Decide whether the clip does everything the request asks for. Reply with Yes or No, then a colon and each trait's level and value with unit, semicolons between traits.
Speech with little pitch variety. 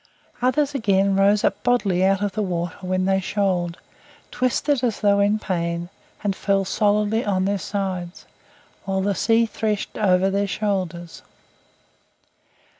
Yes: narrow, 2.2 semitones